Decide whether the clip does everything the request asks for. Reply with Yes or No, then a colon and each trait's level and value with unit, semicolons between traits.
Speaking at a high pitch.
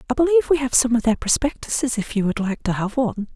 Yes: high, 240 Hz